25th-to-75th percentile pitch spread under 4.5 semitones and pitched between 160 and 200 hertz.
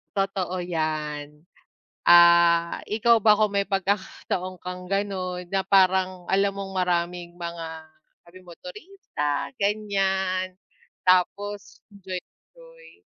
Yes: narrow, 2.4 semitones; medium, 185 Hz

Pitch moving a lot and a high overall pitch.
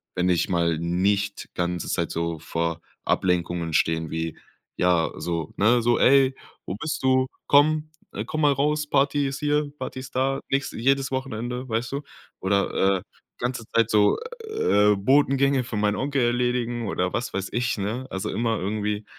No: wide, 6.4 semitones; low, 115 Hz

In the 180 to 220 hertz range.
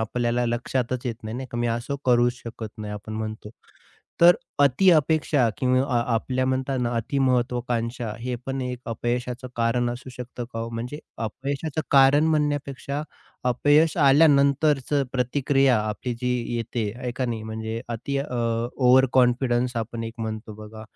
No: low, 125 Hz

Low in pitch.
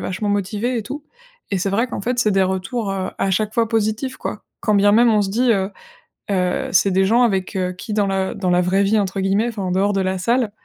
No: high, 205 Hz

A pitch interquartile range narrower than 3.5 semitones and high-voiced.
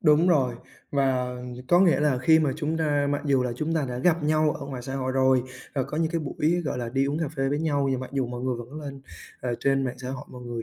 No: average, 3.1 semitones; medium, 140 Hz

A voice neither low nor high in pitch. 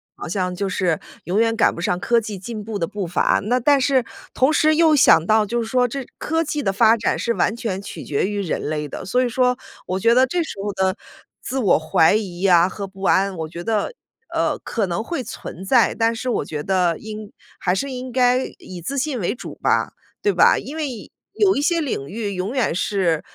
No: high, 215 Hz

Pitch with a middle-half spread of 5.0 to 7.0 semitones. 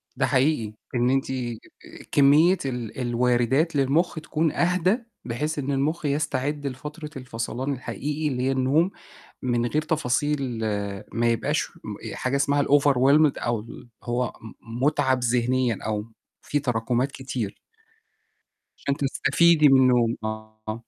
No: average, 3.4 semitones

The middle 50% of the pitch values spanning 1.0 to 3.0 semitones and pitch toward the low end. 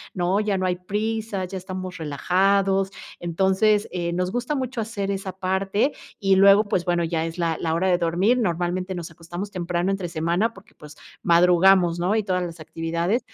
No: narrow, 2.4 semitones; medium, 185 Hz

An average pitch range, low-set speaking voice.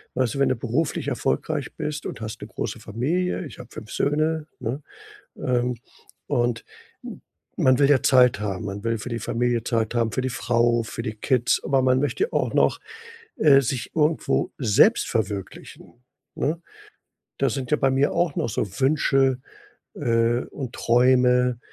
Yes: average, 3.0 semitones; low, 125 Hz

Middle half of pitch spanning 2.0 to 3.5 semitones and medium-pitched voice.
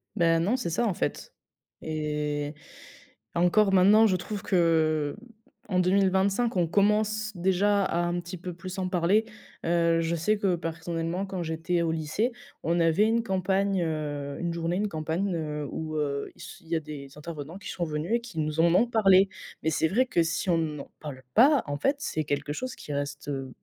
No: average, 3.9 semitones; medium, 170 Hz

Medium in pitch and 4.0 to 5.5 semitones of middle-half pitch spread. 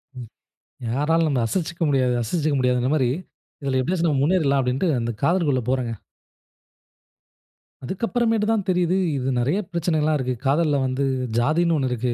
Yes: medium, 145 Hz; average, 5.0 semitones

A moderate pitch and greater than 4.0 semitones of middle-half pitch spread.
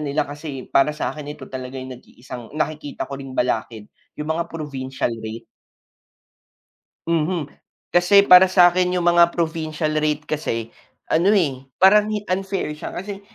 Yes: medium, 155 Hz; average, 4.7 semitones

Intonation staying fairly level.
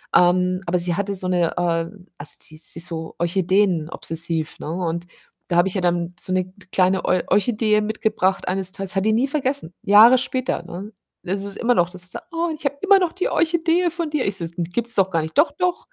No: wide, 5.4 semitones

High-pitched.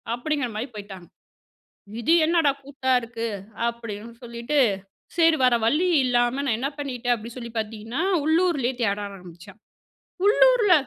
Yes: high, 245 Hz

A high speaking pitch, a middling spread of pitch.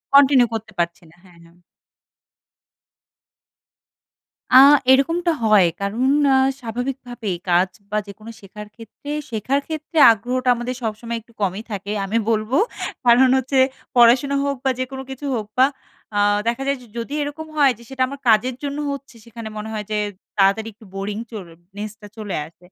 Yes: high, 235 Hz; average, 4.0 semitones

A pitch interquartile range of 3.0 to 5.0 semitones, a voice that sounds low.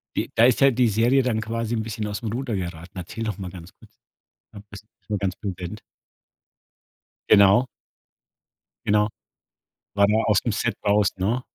No: narrow, 2.6 semitones; low, 105 Hz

